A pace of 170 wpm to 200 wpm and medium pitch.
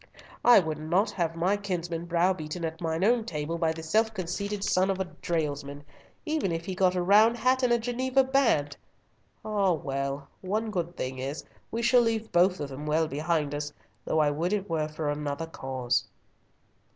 Yes: average, 190 wpm; medium, 170 Hz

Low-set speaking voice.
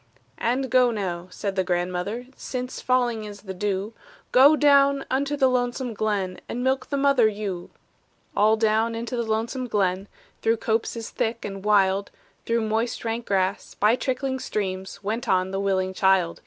No: high, 220 Hz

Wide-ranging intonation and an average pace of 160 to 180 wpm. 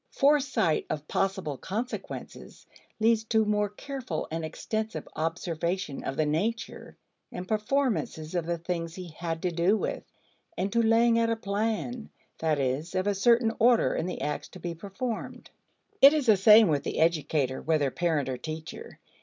Yes: wide, 5.8 semitones; average, 165 wpm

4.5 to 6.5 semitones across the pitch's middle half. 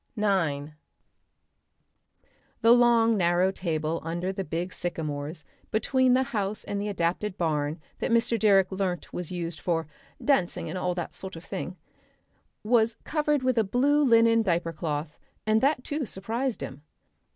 Yes: wide, 5.5 semitones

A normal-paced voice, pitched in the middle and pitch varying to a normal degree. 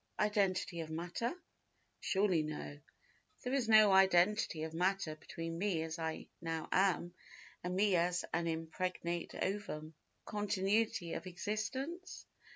No: slow, 125 wpm; medium, 180 Hz; average, 3.9 semitones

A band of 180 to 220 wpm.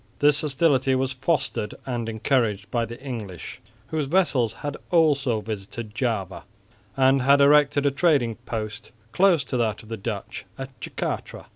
No: average, 150 wpm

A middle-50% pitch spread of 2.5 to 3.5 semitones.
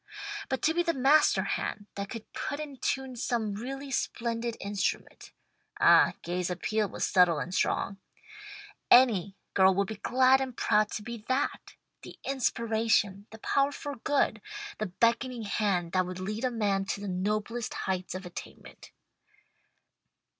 No: average, 4.8 semitones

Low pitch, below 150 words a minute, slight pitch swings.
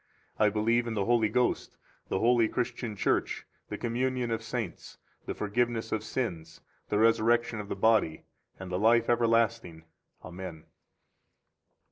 Yes: low, 115 Hz; average, 140 wpm; narrow, 2.3 semitones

